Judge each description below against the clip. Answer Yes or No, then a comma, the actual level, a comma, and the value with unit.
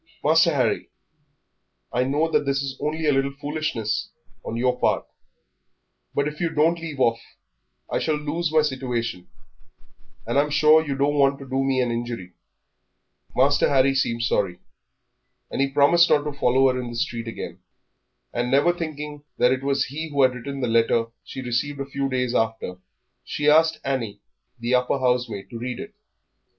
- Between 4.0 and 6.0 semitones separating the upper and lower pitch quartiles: No, average, 3.3 semitones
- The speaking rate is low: No, average, 175 wpm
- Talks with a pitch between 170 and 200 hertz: No, low, 135 Hz